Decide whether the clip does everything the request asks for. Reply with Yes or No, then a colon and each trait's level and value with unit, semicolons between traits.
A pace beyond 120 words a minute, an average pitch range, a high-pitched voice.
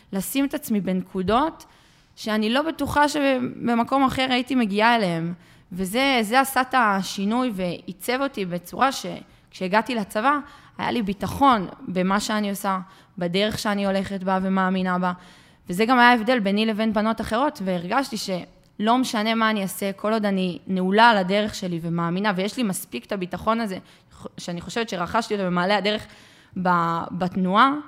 Yes: average, 145 wpm; average, 4.5 semitones; high, 210 Hz